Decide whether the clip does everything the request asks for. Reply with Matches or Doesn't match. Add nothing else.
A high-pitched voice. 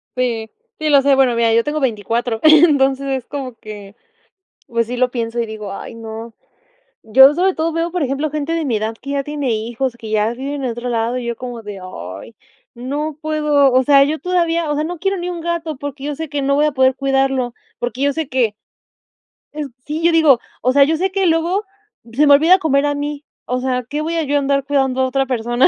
Matches